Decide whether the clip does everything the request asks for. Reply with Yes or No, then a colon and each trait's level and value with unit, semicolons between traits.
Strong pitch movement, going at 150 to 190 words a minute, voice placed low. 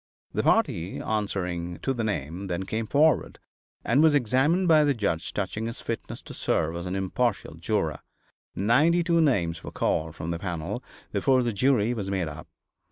Yes: wide, 7.4 semitones; average, 175 wpm; low, 105 Hz